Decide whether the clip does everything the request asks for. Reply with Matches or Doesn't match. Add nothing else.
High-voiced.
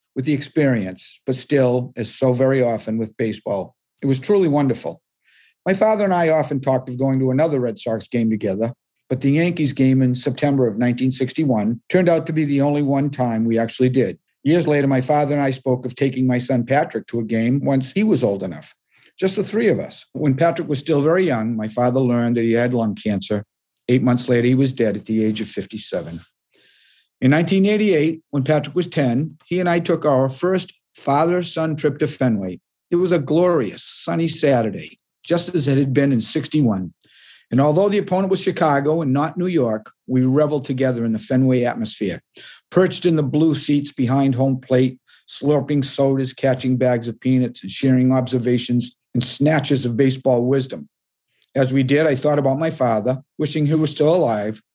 Doesn't match